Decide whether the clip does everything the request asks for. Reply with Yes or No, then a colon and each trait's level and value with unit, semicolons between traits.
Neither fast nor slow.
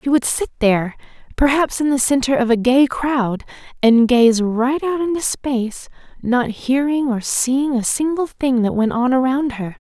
Yes: average, 180 wpm